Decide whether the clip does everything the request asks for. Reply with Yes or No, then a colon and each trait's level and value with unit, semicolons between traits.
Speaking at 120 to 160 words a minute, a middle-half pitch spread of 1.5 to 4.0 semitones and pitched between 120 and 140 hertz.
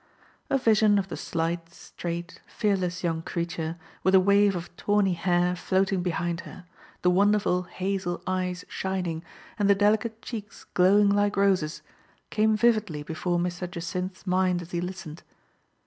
No: average, 150 wpm; narrow, 2.5 semitones; medium, 185 Hz